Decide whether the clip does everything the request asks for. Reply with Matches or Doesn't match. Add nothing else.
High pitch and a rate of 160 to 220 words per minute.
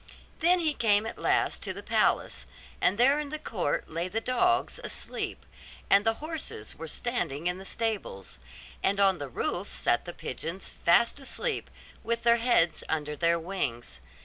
Matches